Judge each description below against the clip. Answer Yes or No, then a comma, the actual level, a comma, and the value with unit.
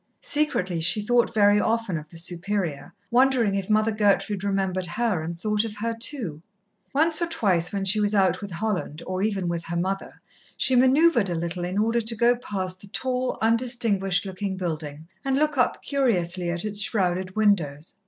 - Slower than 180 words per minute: No, average, 185 wpm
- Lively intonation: No, average, 4.4 semitones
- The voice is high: Yes, high, 200 Hz